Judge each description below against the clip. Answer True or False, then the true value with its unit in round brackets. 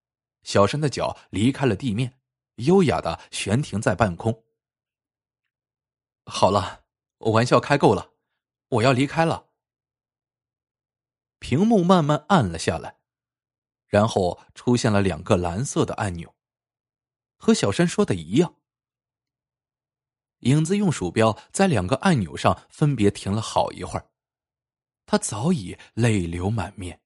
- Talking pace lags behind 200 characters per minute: True (185 characters per minute)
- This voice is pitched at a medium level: False (125 Hz)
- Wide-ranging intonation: True (5.9 semitones)